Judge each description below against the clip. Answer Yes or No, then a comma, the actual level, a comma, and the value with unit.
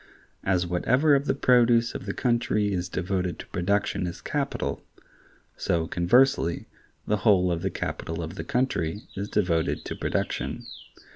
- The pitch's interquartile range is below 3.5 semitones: No, wide, 5.6 semitones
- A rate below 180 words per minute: Yes, average, 150 wpm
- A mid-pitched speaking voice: No, low, 100 Hz